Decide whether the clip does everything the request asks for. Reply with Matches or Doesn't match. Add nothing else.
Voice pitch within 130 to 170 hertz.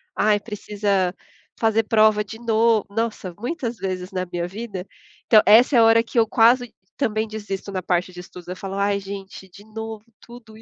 Doesn't match